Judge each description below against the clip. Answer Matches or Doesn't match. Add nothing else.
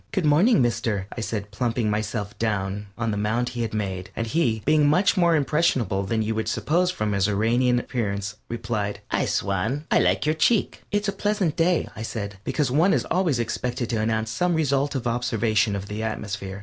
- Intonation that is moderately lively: Doesn't match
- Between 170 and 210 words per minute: Matches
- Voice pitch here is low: Matches